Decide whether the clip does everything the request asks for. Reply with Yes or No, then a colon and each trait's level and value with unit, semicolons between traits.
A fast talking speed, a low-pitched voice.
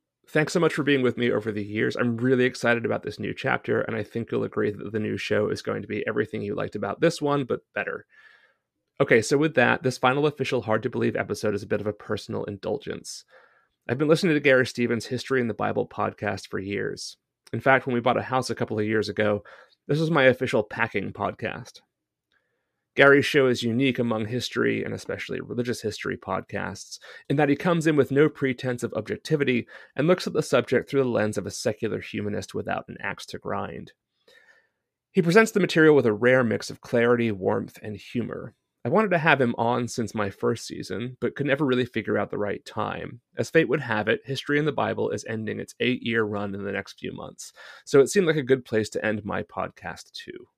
Yes: fast, 225 wpm; low, 125 Hz